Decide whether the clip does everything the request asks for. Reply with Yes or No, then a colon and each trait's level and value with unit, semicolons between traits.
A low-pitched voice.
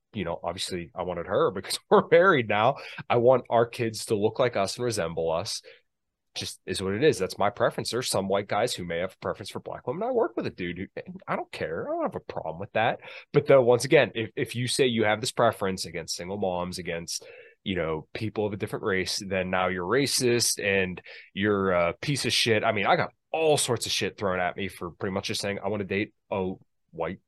Yes: low, 110 Hz